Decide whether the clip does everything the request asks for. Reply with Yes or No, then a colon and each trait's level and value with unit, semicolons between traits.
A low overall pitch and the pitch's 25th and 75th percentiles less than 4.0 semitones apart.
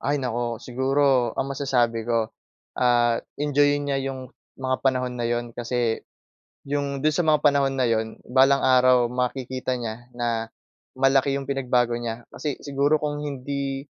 Yes: low, 130 Hz; narrow, 2.6 semitones